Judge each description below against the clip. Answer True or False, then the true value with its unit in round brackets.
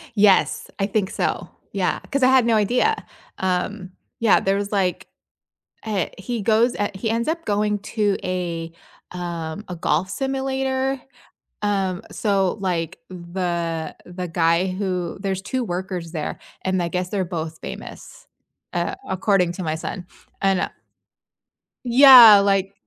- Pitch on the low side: False (190 Hz)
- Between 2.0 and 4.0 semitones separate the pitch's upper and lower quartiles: True (3.3 semitones)